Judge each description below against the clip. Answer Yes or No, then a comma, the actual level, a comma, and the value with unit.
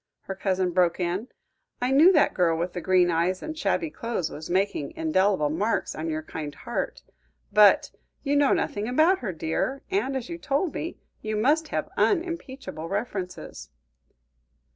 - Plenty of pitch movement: Yes, wide, 8.4 semitones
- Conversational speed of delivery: Yes, average, 165 wpm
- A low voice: No, high, 210 Hz